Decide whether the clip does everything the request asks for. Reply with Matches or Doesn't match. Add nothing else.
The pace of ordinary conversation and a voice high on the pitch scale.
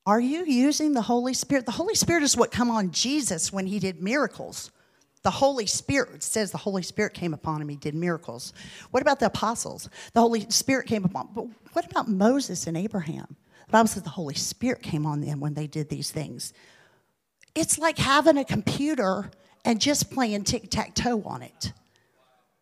Matches